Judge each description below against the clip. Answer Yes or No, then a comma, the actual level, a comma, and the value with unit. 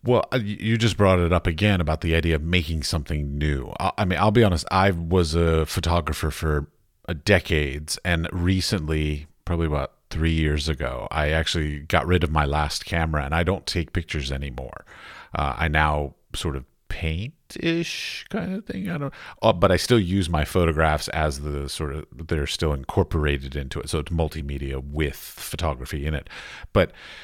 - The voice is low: Yes, very low, 80 Hz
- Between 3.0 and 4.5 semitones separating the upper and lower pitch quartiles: Yes, average, 3.7 semitones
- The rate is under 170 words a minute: No, average, 180 wpm